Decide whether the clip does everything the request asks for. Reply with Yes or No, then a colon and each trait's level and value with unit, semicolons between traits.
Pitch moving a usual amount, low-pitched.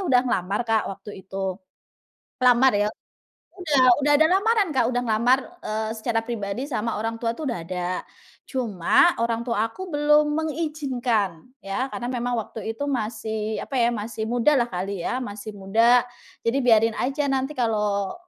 No: average, 3.7 semitones; high, 235 Hz